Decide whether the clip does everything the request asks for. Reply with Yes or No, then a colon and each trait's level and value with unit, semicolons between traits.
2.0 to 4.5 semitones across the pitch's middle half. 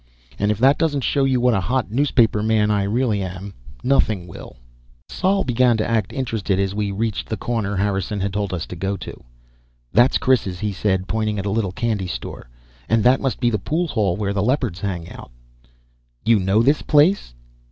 Yes: average, 4.1 semitones